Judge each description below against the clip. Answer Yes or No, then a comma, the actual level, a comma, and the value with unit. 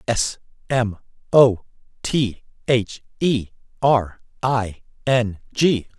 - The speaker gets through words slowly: Yes, slow, 100 wpm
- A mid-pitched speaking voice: No, low, 120 Hz